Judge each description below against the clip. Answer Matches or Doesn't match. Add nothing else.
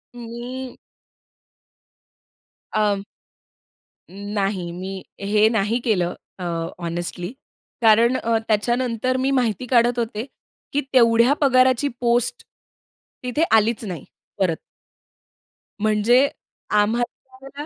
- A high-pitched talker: Matches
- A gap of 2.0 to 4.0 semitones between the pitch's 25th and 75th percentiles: Matches